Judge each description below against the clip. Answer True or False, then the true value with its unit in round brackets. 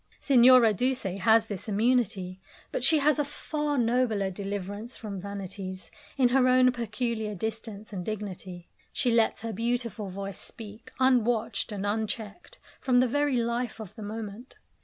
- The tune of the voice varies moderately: True (3.6 semitones)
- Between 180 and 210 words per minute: False (150 wpm)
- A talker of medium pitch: False (225 Hz)